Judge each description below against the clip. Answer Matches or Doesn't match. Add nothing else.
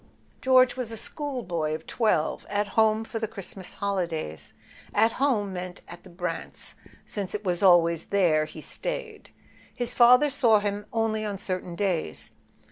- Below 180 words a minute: Matches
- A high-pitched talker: Matches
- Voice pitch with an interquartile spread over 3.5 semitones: Matches